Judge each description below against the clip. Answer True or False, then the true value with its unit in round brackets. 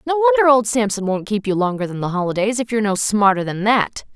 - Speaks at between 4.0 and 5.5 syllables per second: False (6.5 syllables/s)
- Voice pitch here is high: True (215 Hz)